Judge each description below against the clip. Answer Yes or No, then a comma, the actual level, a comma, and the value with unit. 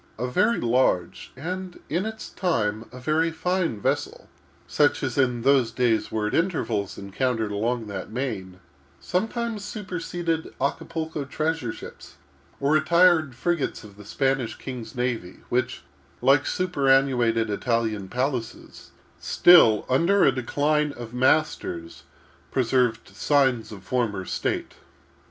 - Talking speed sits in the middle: No, slow, 125 wpm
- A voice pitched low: Yes, low, 130 Hz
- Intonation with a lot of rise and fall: Yes, wide, 6.0 semitones